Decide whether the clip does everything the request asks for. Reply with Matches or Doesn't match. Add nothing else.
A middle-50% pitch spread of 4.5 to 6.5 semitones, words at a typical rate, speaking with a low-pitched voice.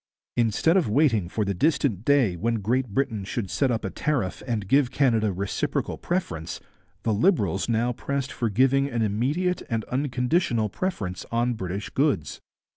Matches